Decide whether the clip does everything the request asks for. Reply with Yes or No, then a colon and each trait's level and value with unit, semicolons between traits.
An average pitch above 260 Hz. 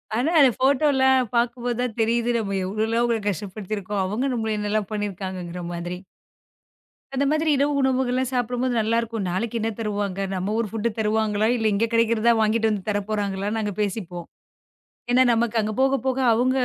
No: high, 220 Hz